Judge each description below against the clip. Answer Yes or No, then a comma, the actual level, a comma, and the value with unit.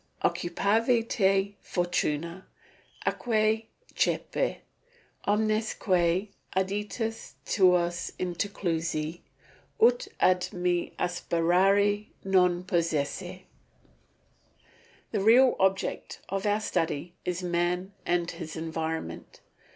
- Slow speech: Yes, slow, 80 wpm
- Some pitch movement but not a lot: Yes, average, 3.0 semitones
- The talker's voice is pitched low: No, medium, 185 Hz